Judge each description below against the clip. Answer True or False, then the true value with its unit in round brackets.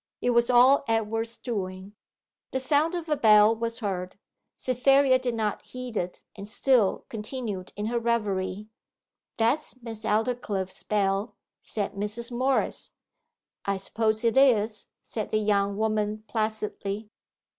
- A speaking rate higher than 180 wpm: False (135 wpm)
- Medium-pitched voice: False (220 Hz)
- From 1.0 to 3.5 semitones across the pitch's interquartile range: True (2.9 semitones)